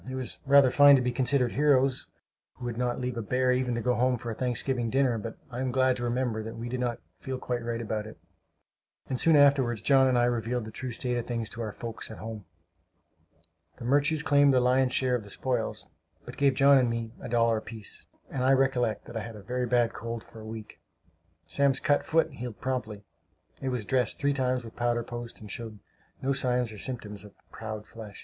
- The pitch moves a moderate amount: No, narrow, 2.3 semitones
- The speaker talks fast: Yes, fast, 225 wpm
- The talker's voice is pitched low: Yes, low, 125 Hz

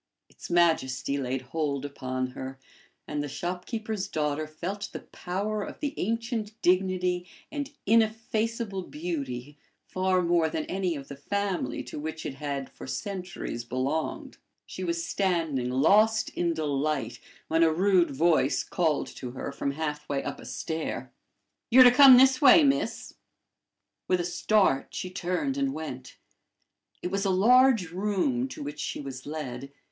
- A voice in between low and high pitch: Yes, medium, 175 Hz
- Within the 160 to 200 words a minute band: No, average, 150 wpm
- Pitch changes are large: Yes, wide, 6.0 semitones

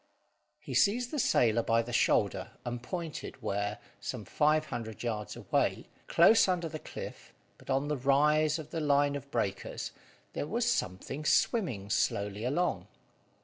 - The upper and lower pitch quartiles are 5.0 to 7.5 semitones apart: Yes, wide, 5.5 semitones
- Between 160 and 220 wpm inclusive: No, average, 150 wpm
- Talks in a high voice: No, medium, 140 Hz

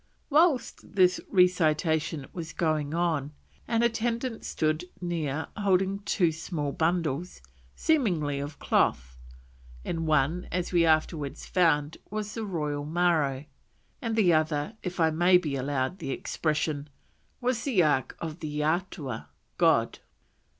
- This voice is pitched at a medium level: Yes, medium, 165 Hz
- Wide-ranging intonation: No, average, 3.7 semitones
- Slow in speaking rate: Yes, slow, 130 wpm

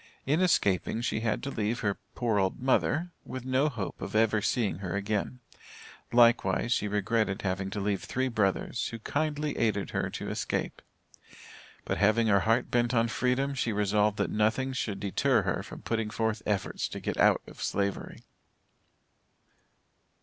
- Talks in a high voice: No, low, 110 Hz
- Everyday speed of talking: Yes, average, 165 wpm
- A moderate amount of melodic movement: Yes, average, 3.4 semitones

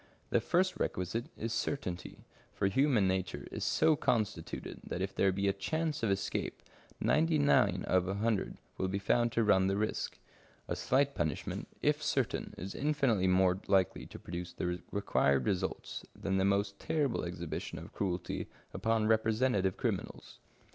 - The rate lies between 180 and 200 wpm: No, average, 160 wpm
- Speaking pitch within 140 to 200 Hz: No, low, 100 Hz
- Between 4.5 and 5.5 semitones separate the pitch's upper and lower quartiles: No, average, 3.9 semitones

